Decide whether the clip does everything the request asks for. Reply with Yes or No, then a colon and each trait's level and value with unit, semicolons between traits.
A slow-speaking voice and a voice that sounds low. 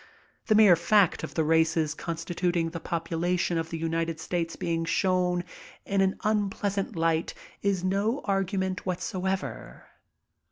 No: slow, 130 wpm; medium, 180 Hz